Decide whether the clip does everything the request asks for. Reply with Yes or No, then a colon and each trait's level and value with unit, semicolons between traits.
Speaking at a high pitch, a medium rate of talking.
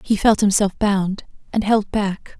Yes: high, 205 Hz; average, 175 wpm